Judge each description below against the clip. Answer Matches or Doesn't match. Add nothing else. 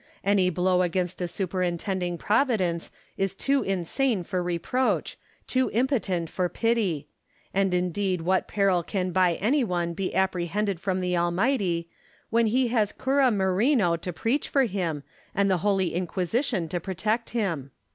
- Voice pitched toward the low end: Doesn't match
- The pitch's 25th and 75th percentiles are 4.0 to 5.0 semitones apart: Doesn't match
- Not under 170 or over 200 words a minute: Doesn't match